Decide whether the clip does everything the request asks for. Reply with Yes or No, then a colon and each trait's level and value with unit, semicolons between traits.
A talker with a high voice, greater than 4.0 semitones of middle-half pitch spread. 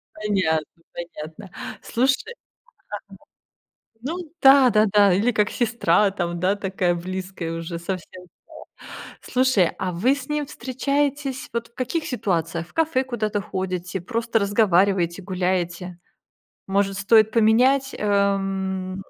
Yes: high, 200 Hz; average, 4.8 semitones